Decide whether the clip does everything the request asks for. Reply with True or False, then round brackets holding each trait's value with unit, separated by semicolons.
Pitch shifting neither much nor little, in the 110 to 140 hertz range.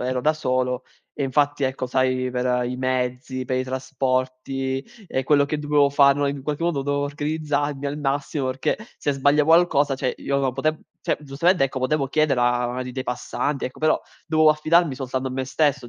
False (2.3 semitones; 135 Hz)